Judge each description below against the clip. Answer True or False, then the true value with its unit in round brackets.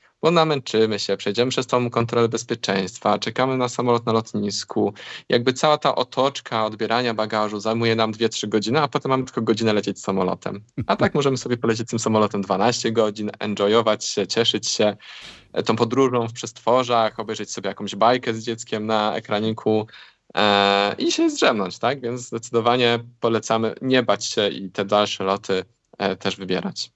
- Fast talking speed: True (165 wpm)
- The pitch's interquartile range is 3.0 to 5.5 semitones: False (2.5 semitones)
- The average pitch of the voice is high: False (115 Hz)